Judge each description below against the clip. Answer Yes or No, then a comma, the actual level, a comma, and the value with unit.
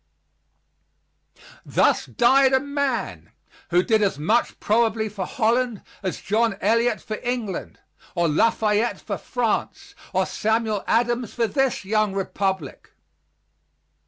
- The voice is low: No, high, 220 Hz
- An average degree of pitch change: Yes, average, 3.3 semitones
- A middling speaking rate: No, slow, 115 wpm